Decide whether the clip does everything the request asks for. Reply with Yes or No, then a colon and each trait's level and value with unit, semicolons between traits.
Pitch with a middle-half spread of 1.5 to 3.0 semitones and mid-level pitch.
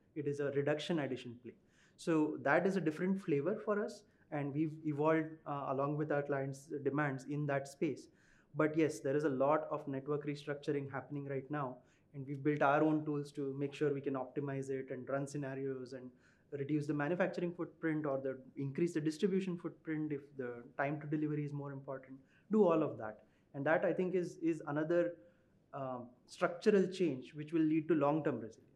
Yes: narrow, 2.5 semitones; medium, 145 Hz